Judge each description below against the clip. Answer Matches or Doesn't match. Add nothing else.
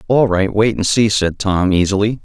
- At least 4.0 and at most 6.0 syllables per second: Matches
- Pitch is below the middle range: Matches